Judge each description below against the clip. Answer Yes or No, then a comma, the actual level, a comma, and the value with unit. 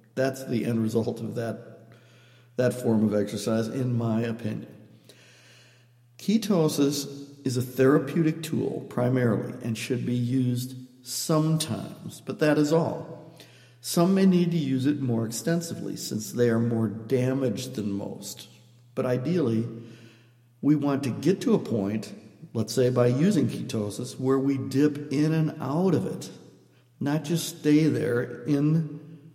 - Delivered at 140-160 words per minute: Yes, average, 145 wpm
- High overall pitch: No, low, 130 Hz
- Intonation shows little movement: No, average, 4.4 semitones